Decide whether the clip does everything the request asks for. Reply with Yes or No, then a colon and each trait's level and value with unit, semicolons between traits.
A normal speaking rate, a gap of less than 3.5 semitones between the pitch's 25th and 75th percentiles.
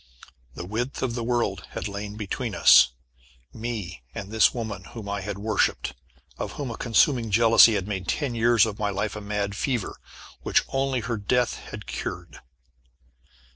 Yes: average, 170 wpm; average, 2.9 semitones